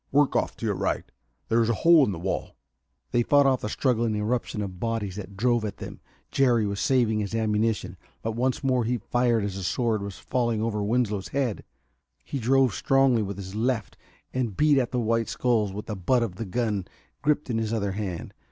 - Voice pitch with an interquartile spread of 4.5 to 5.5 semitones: No, average, 3.3 semitones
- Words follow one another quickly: Yes, fast, 210 wpm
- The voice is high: No, low, 115 Hz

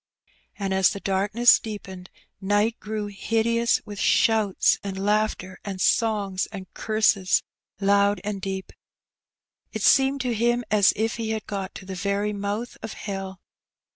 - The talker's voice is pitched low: No, high, 205 Hz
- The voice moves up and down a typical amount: No, narrow, 2.3 semitones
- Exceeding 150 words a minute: No, average, 145 wpm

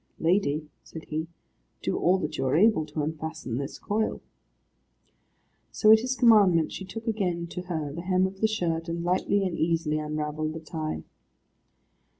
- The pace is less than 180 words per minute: Yes, average, 165 wpm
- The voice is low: No, medium, 165 Hz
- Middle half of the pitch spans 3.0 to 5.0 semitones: Yes, average, 3.7 semitones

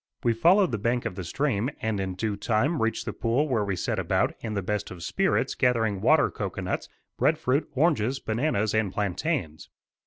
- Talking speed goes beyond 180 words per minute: Yes, average, 190 wpm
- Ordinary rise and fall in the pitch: Yes, average, 4.6 semitones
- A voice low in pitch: Yes, low, 110 Hz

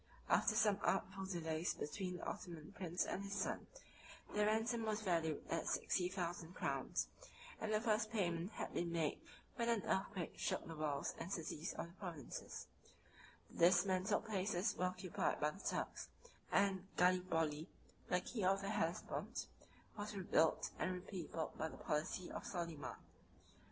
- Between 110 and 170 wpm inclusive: Yes, average, 155 wpm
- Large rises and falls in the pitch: No, average, 3.2 semitones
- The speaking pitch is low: No, medium, 185 Hz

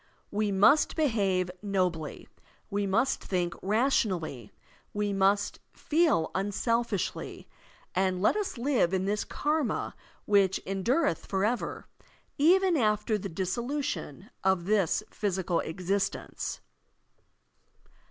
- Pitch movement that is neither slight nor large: Yes, average, 4.1 semitones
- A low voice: No, high, 200 Hz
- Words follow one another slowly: Yes, slow, 100 wpm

